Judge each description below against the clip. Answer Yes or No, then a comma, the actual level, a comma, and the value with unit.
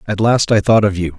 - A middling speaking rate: No, fast, 305 wpm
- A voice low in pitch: Yes, low, 100 Hz